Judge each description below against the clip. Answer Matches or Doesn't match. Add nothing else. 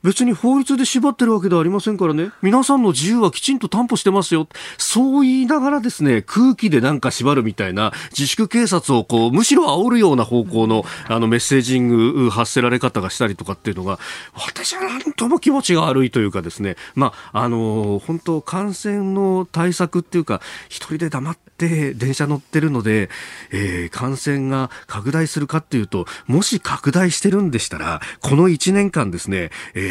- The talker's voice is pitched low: Doesn't match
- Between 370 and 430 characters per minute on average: Matches